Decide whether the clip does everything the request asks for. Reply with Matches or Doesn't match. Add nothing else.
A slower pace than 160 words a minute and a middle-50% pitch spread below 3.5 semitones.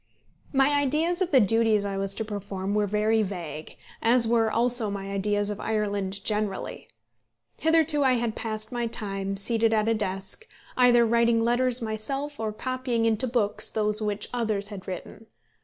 Doesn't match